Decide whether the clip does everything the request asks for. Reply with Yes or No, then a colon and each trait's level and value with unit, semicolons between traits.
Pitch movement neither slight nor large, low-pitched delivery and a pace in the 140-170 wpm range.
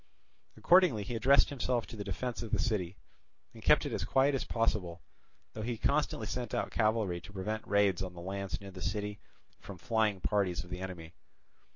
No: average, 3.5 semitones; low, 105 Hz; average, 195 wpm